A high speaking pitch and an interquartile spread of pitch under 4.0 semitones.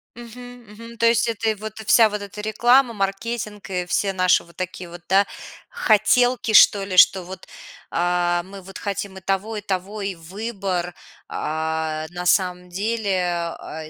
Yes: high, 195 Hz; average, 3.4 semitones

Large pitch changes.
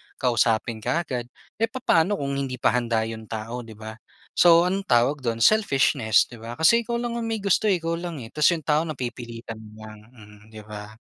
Yes: wide, 7.2 semitones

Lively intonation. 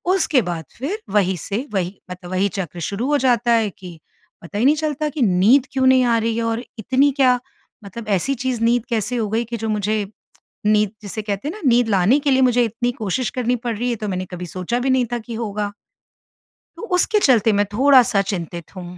No: average, 4.2 semitones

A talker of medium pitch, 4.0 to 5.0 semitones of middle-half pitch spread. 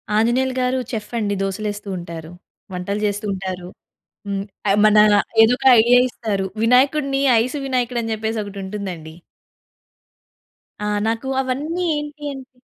No: high, 220 Hz; average, 4.4 semitones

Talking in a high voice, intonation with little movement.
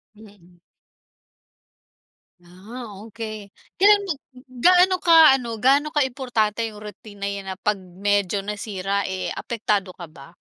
No: high, 210 Hz; average, 4.2 semitones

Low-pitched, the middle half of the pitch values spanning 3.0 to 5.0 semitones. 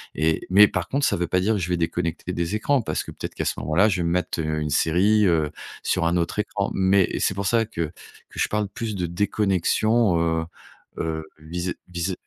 Yes: very low, 90 Hz; average, 3.7 semitones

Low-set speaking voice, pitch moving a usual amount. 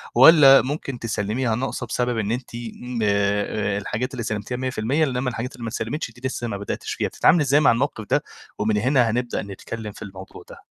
Yes: low, 120 Hz; average, 3.2 semitones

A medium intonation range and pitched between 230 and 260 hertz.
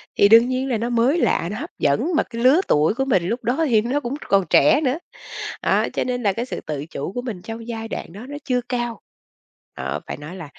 Yes: average, 4.3 semitones; high, 235 Hz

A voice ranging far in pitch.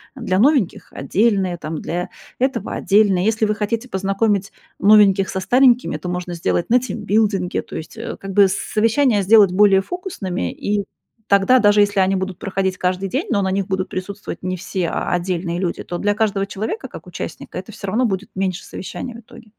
No: average, 2.7 semitones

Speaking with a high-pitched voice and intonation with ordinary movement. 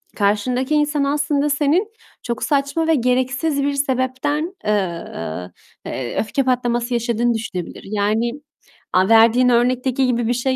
Yes: very high, 250 Hz; average, 3.8 semitones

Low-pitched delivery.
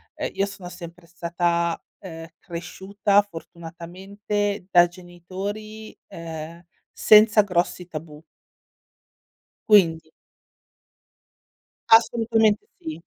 No: medium, 180 Hz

